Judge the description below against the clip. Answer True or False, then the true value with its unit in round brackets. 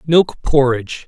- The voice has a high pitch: False (140 Hz)